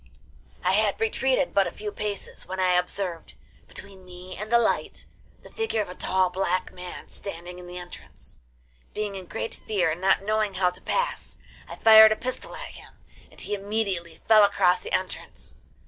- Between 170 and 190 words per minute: Yes, average, 185 wpm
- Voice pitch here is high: Yes, high, 195 Hz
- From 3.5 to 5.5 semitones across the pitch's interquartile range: No, average, 3.0 semitones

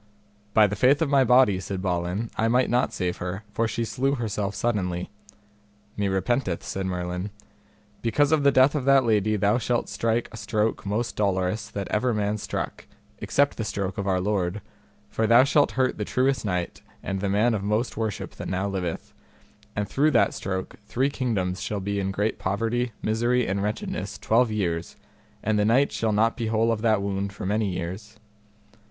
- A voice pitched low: Yes, low, 105 Hz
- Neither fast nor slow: Yes, average, 190 wpm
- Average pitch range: Yes, average, 3.6 semitones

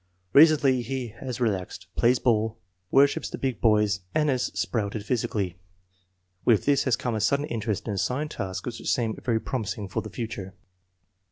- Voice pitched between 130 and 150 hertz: No, low, 115 Hz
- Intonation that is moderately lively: Yes, average, 3.7 semitones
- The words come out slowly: No, average, 170 wpm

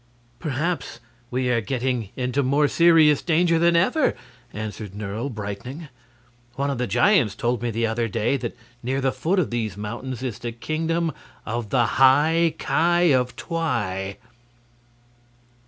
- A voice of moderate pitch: No, low, 130 Hz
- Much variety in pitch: Yes, wide, 5.7 semitones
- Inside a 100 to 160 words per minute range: Yes, average, 145 wpm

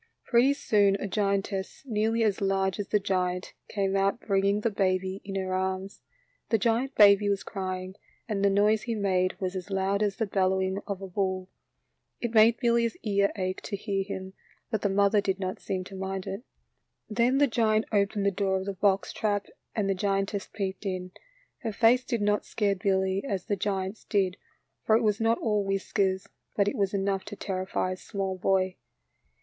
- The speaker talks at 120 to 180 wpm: No, average, 200 wpm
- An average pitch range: No, narrow, 1.7 semitones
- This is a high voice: Yes, high, 195 Hz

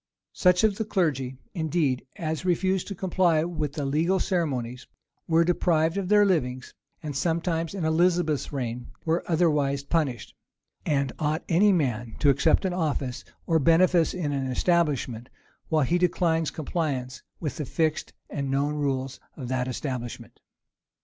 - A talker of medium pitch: Yes, medium, 155 Hz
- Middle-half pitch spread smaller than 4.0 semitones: No, average, 4.3 semitones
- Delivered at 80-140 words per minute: No, average, 150 wpm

